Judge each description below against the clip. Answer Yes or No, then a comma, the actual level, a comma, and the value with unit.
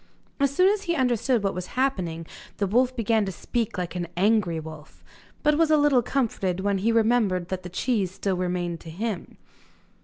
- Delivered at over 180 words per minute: Yes, average, 190 wpm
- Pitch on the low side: No, high, 205 Hz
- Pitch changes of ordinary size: No, wide, 5.7 semitones